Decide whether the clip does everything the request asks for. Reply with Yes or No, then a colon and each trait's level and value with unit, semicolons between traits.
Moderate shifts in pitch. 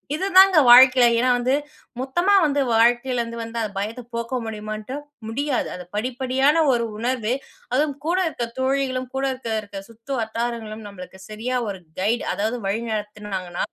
Yes: average, 3.4 semitones